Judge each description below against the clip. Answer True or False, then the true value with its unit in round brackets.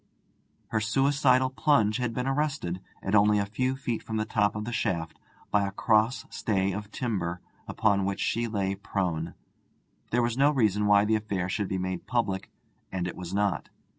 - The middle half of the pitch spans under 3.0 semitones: False (3.6 semitones)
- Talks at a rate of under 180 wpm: False (185 wpm)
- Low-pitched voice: True (105 Hz)